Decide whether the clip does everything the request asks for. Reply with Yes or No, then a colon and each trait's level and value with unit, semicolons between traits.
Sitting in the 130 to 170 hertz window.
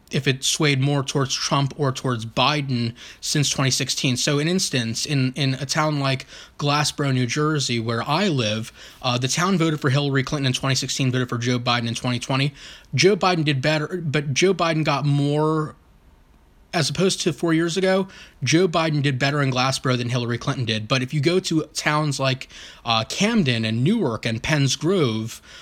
Yes: medium, 140 Hz